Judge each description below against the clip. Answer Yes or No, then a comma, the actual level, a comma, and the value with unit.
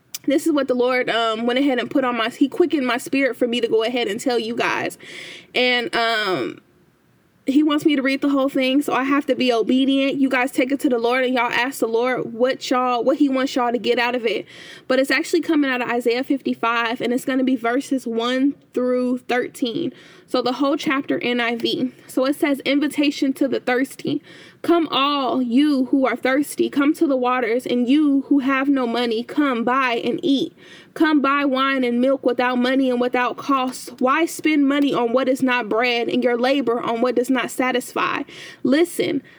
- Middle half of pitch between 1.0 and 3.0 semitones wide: Yes, narrow, 2.4 semitones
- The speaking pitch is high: Yes, very high, 260 Hz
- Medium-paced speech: No, fast, 215 wpm